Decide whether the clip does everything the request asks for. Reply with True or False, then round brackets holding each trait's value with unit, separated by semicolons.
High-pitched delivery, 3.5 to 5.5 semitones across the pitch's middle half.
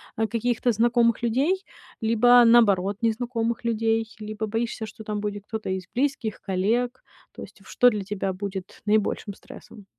False (225 Hz; 2.5 semitones)